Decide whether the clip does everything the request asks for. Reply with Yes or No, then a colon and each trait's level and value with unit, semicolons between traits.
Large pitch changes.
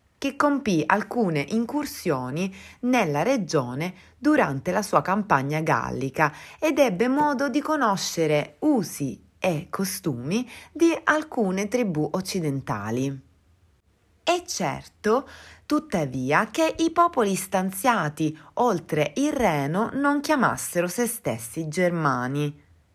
Yes: wide, 9.0 semitones